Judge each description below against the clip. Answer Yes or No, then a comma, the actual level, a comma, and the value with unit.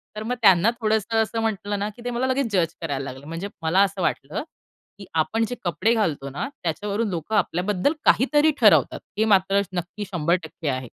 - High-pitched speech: Yes, high, 200 Hz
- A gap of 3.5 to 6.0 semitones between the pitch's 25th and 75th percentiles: Yes, average, 5.0 semitones